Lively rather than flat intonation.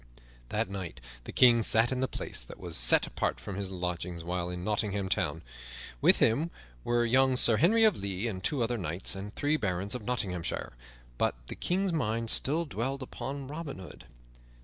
Yes: wide, 6.1 semitones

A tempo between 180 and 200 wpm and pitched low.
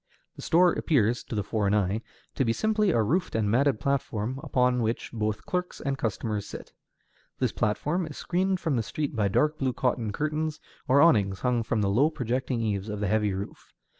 Yes: average, 195 wpm; low, 120 Hz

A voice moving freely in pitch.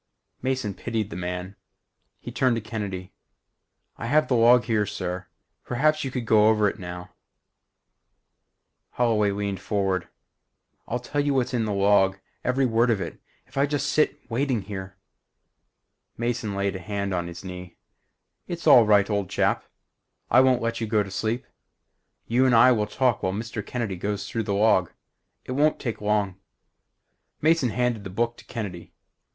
No: average, 3.9 semitones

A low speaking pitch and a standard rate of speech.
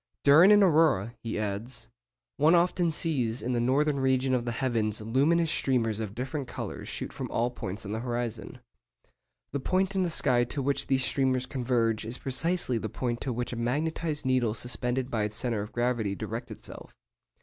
Yes: low, 125 Hz; average, 185 wpm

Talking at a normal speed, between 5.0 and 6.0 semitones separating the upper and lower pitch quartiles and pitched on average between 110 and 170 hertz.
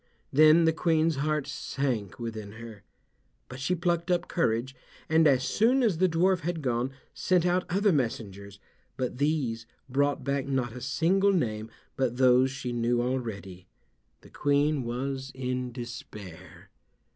Yes: average, 145 wpm; average, 5.3 semitones; low, 135 Hz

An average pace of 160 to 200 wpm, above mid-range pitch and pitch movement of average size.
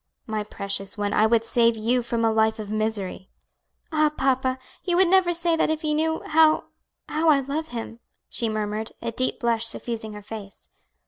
No: average, 190 wpm; high, 235 Hz; wide, 6.0 semitones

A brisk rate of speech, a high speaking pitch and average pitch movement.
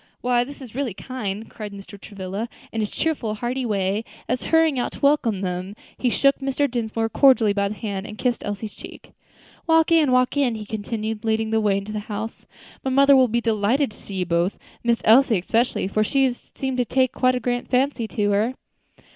Yes: fast, 210 wpm; high, 225 Hz; average, 3.7 semitones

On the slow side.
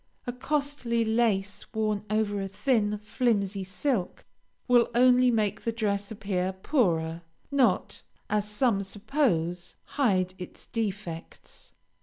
Yes: slow, 115 wpm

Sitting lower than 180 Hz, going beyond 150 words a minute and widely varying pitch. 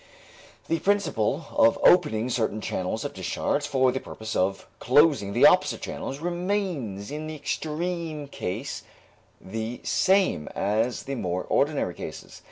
No: low, 135 Hz; average, 140 wpm; wide, 6.7 semitones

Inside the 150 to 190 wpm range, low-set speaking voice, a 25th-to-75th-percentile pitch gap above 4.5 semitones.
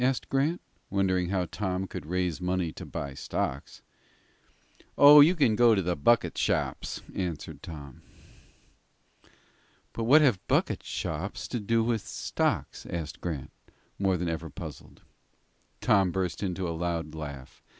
No: average, 140 wpm; very low, 90 Hz; average, 5.2 semitones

